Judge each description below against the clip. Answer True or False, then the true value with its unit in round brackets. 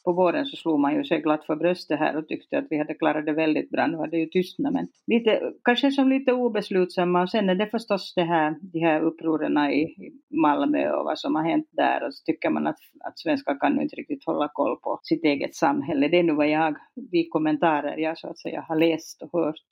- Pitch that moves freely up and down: True (9.0 semitones)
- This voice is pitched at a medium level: True (175 Hz)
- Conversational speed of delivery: False (245 wpm)